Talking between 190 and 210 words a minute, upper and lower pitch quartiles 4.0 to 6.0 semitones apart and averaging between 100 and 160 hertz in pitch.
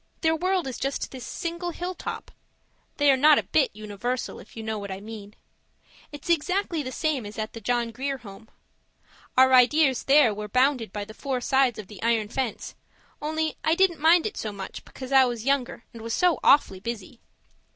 No: average, 195 wpm; wide, 5.5 semitones; very high, 255 Hz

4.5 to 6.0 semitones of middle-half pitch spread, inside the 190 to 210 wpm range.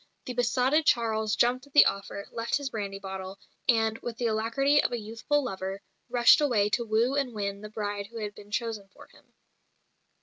No: average, 3.2 semitones; average, 195 wpm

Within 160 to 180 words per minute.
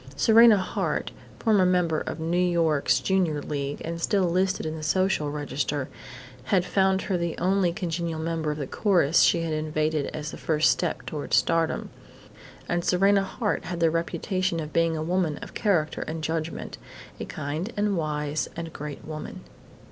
Yes: average, 170 wpm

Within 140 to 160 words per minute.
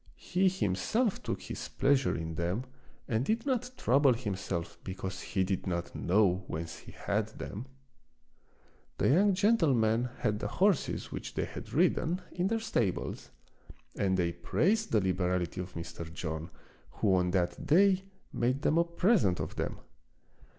Yes: average, 155 wpm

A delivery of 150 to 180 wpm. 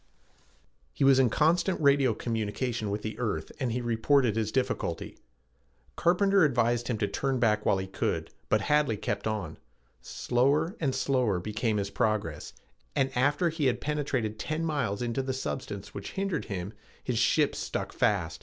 Yes: average, 165 wpm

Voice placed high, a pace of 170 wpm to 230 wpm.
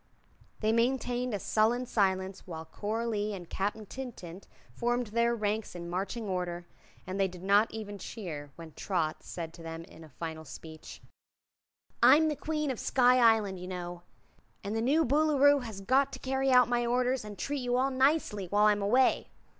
Yes: high, 215 Hz; average, 180 wpm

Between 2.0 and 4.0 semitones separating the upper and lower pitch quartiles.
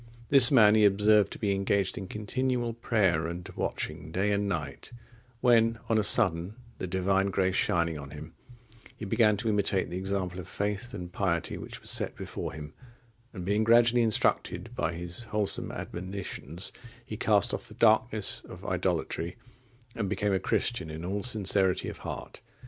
Yes: average, 3.5 semitones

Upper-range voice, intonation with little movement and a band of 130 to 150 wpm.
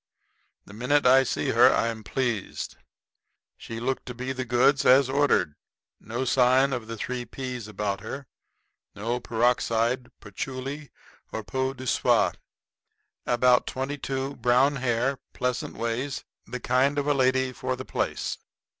No: low, 125 Hz; narrow, 2.3 semitones; average, 145 wpm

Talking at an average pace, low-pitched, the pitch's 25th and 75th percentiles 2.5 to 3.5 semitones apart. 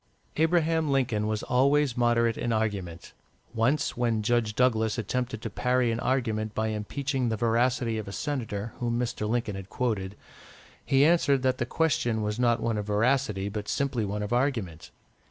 Yes: average, 170 wpm; low, 115 Hz; average, 3.2 semitones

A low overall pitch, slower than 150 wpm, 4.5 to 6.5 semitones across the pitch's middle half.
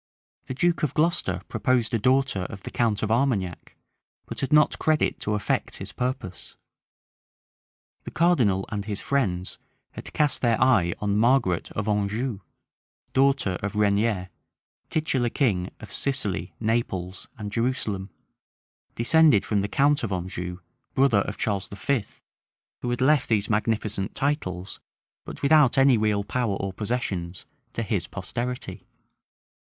Yes: low, 110 Hz; average, 140 wpm; average, 4.9 semitones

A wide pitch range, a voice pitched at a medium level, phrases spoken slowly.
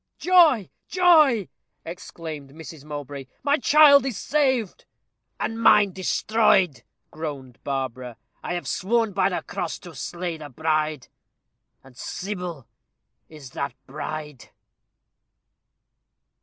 Yes: wide, 7.5 semitones; medium, 170 Hz; slow, 105 wpm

